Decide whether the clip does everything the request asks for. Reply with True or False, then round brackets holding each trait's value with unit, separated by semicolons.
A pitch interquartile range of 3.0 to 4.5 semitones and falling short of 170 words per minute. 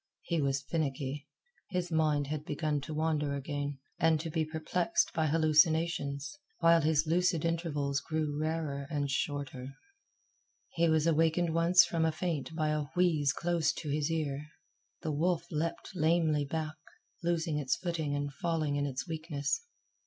False (2.4 semitones; 150 wpm)